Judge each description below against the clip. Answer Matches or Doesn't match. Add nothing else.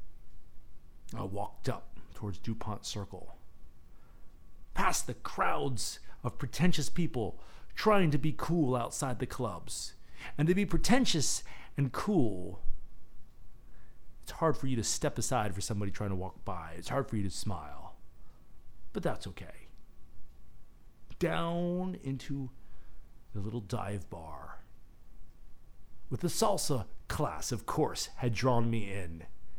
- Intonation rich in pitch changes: Matches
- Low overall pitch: Matches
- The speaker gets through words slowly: Matches